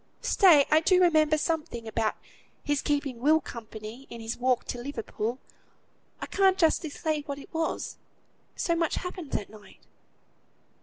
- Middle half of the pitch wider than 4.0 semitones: Yes, wide, 5.4 semitones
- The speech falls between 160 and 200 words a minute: No, average, 150 wpm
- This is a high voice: Yes, very high, 290 Hz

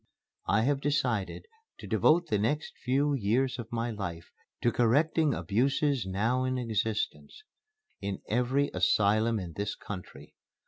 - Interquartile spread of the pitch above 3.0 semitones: Yes, average, 5.0 semitones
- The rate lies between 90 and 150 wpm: Yes, slow, 135 wpm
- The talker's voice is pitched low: Yes, low, 120 Hz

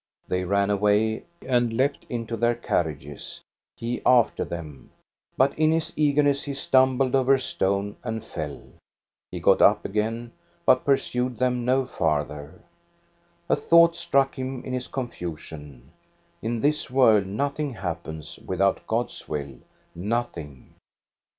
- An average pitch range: No, wide, 6.2 semitones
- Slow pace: Yes, slow, 130 wpm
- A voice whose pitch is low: Yes, low, 115 Hz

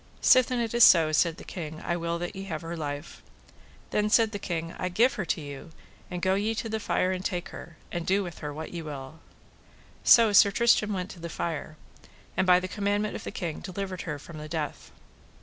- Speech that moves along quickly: Yes, fast, 225 wpm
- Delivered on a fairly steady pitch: No, average, 4.0 semitones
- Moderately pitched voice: Yes, medium, 180 Hz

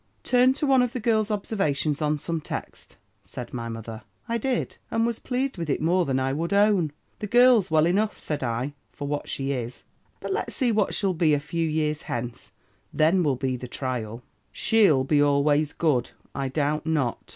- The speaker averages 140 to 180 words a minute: No, average, 195 wpm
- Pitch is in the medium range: Yes, medium, 155 Hz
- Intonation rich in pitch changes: Yes, wide, 7.5 semitones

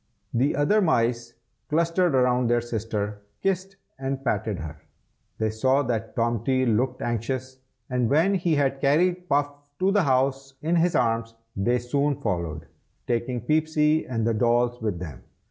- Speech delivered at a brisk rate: No, average, 160 wpm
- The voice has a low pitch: Yes, low, 130 Hz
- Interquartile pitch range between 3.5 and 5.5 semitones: Yes, average, 4.1 semitones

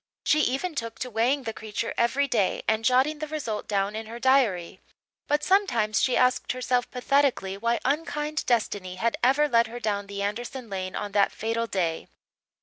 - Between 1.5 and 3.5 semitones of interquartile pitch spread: No, average, 4.3 semitones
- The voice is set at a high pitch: Yes, high, 235 Hz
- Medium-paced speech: Yes, average, 180 wpm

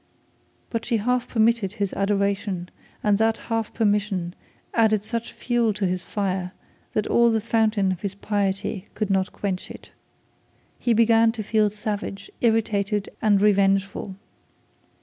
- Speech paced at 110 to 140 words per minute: Yes, slow, 135 wpm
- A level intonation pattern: Yes, narrow, 2.2 semitones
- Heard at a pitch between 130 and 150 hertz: No, high, 210 Hz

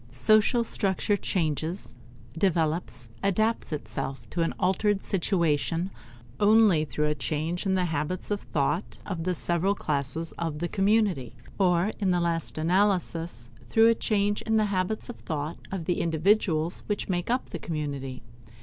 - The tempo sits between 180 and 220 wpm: No, average, 150 wpm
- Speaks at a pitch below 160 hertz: No, medium, 175 Hz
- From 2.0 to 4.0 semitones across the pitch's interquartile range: No, average, 4.4 semitones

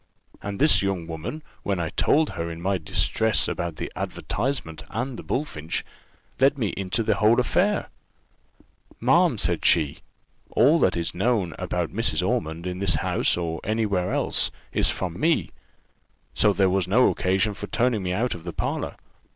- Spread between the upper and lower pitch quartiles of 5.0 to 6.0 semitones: Yes, wide, 5.6 semitones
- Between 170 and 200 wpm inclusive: Yes, average, 175 wpm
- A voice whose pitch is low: Yes, very low, 95 Hz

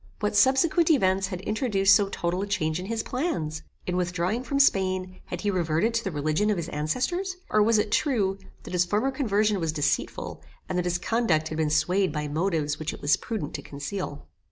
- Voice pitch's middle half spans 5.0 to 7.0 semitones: Yes, average, 5.3 semitones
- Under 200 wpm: No, fast, 205 wpm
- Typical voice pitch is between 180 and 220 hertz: Yes, high, 190 Hz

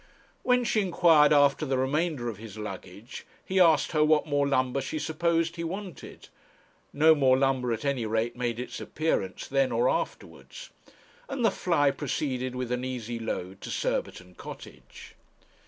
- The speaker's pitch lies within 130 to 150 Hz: Yes, low, 135 Hz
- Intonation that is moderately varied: Yes, average, 4.9 semitones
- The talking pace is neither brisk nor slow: Yes, average, 160 wpm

